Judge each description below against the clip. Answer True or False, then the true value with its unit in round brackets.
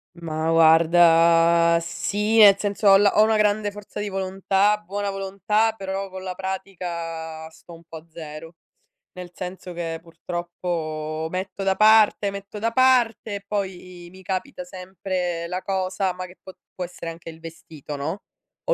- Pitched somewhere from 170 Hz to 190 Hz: True (185 Hz)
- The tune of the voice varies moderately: True (3.1 semitones)